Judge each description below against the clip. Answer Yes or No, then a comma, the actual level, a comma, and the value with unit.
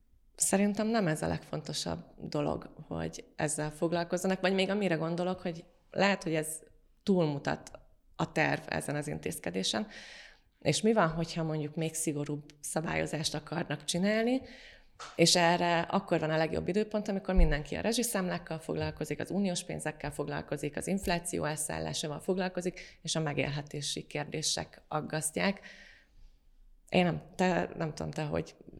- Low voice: No, medium, 165 Hz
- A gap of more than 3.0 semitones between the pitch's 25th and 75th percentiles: Yes, average, 3.5 semitones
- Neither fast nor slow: Yes, average, 135 wpm